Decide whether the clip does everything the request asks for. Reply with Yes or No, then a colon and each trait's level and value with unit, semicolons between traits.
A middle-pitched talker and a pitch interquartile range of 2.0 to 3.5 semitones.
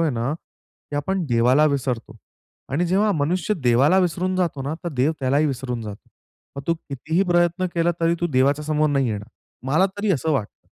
No: medium, 150 Hz; average, 4.7 semitones